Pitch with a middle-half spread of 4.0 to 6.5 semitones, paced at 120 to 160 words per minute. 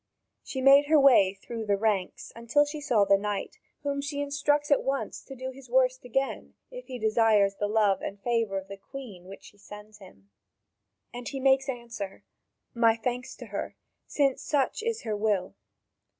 No: average, 4.9 semitones; average, 180 wpm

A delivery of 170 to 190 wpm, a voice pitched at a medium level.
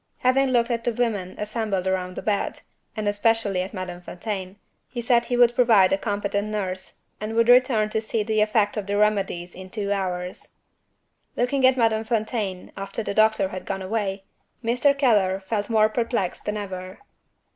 No: average, 180 wpm; high, 210 Hz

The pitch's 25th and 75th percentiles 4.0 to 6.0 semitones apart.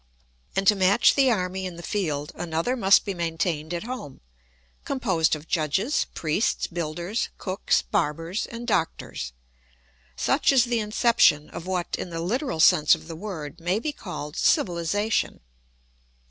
Yes: average, 4.7 semitones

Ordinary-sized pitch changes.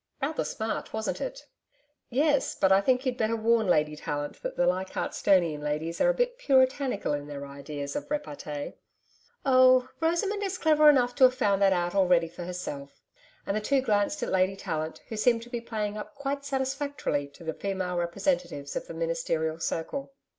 No: wide, 8.1 semitones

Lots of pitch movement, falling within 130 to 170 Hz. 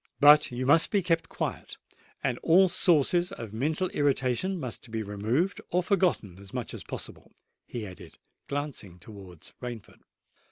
Yes: wide, 7.5 semitones; low, 135 Hz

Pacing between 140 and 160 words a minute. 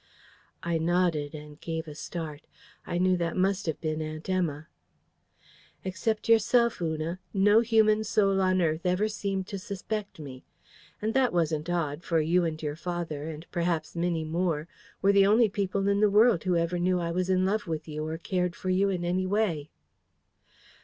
No: average, 180 wpm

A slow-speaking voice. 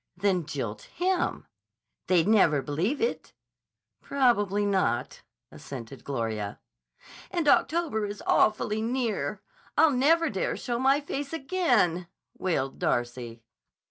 Yes: slow, 110 wpm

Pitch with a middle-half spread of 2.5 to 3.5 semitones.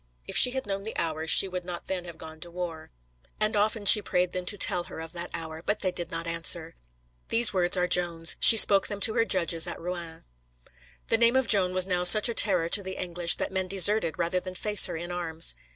Yes: average, 3.2 semitones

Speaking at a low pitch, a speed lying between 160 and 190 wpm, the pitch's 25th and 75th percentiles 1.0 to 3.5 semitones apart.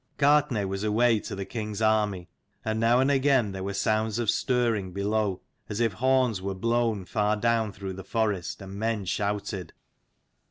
Yes: low, 110 Hz; average, 170 wpm; average, 3.0 semitones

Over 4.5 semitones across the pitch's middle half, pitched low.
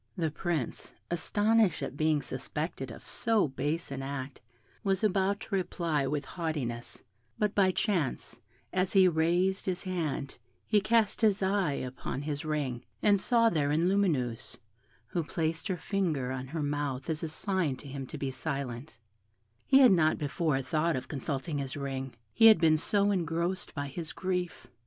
No: average, 5.2 semitones; medium, 160 Hz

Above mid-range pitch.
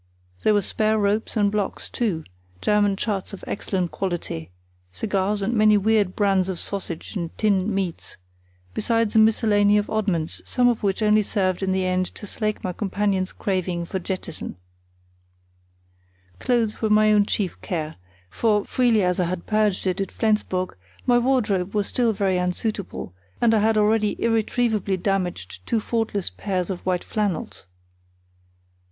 Yes: high, 205 Hz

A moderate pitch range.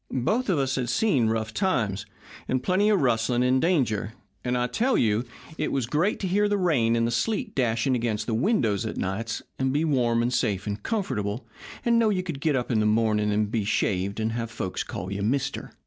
No: wide, 6.7 semitones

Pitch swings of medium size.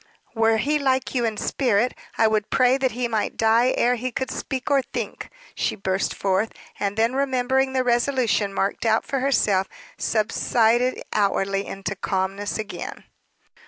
Yes: average, 4.0 semitones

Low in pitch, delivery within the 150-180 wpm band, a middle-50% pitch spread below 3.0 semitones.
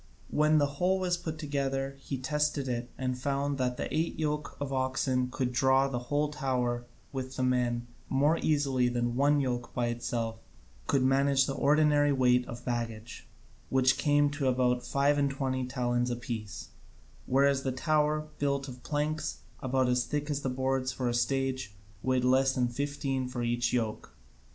Yes: low, 130 Hz; average, 170 wpm; narrow, 2.4 semitones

